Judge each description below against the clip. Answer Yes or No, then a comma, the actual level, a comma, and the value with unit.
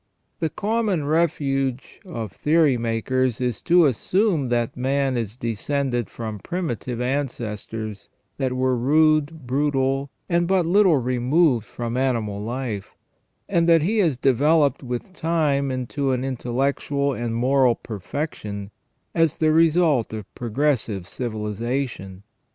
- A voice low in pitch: Yes, low, 130 Hz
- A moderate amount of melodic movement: Yes, average, 4.6 semitones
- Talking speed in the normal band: No, slow, 120 wpm